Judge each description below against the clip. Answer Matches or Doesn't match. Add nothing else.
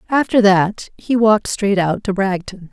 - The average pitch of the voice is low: Doesn't match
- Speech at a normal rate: Matches